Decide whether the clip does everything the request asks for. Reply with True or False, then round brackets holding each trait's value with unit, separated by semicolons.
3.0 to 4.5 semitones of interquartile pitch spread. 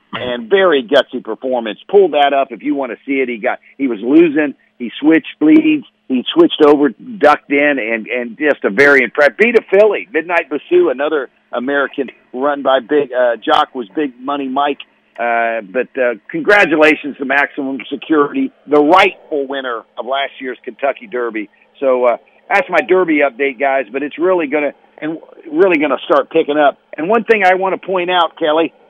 False (5.1 semitones)